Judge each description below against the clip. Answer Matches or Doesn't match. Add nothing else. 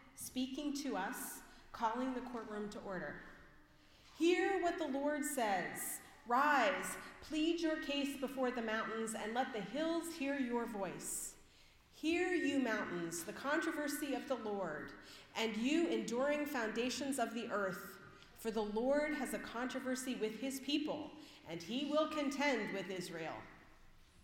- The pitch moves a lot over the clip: Matches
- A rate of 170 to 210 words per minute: Doesn't match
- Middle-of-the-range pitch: Doesn't match